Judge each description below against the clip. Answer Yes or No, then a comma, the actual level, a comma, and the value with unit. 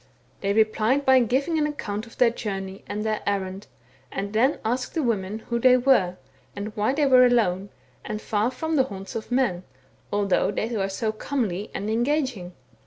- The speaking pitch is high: Yes, high, 220 Hz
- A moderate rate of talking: Yes, average, 185 wpm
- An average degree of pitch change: Yes, average, 4.2 semitones